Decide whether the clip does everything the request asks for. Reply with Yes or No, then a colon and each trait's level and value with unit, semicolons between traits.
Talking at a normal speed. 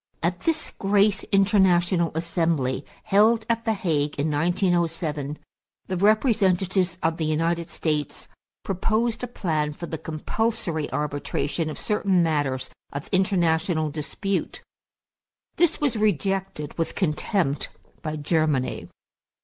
No: slow, 115 wpm